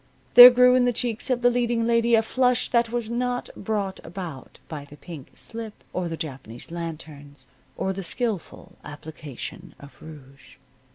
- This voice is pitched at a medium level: No, high, 195 Hz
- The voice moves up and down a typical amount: No, wide, 7.5 semitones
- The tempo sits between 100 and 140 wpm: No, average, 165 wpm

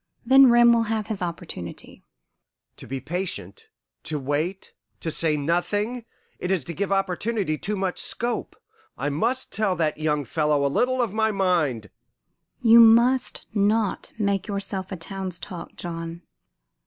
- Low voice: No, high, 190 Hz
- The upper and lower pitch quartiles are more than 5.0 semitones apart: Yes, wide, 5.4 semitones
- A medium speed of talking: Yes, average, 155 wpm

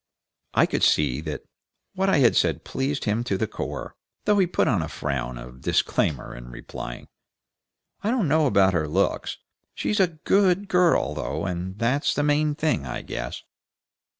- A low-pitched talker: Yes, low, 115 Hz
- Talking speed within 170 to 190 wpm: Yes, average, 175 wpm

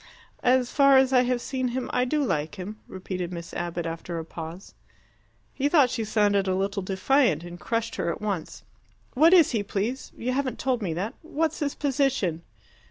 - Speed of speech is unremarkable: Yes, average, 190 wpm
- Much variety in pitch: Yes, wide, 6.3 semitones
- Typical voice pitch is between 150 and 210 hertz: No, high, 225 Hz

